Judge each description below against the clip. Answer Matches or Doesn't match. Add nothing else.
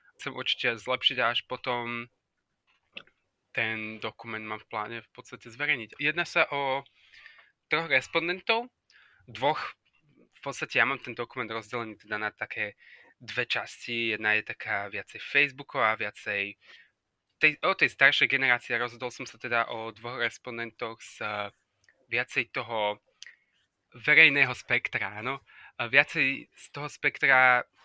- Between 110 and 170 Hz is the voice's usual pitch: Matches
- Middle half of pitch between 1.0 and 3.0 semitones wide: Doesn't match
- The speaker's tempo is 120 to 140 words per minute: Matches